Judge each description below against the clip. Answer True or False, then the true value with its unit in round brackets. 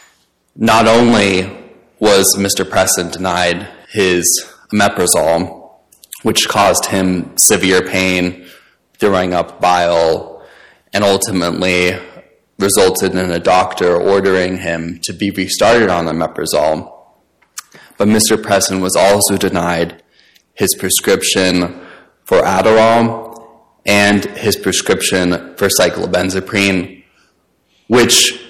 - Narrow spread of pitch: True (1.8 semitones)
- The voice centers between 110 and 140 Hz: False (95 Hz)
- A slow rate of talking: True (95 wpm)